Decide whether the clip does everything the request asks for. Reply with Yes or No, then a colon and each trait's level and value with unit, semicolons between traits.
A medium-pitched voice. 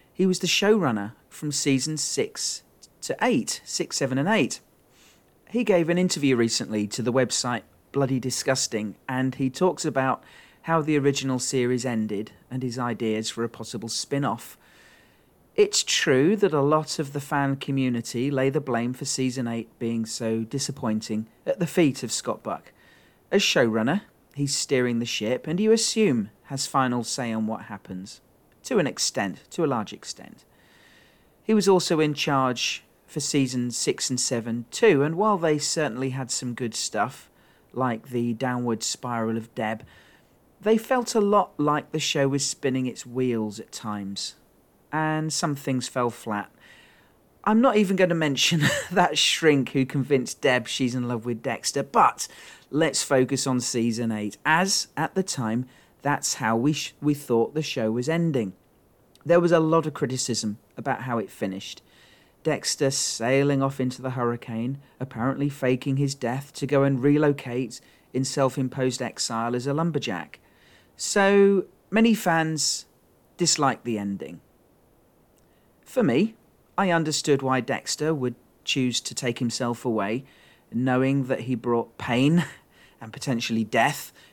No: low, 130 Hz